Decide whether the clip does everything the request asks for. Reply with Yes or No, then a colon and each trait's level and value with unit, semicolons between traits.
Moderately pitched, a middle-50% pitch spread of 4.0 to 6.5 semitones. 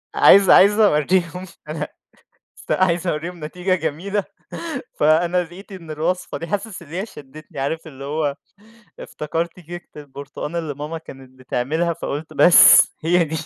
No: medium, 165 Hz; average, 3.2 semitones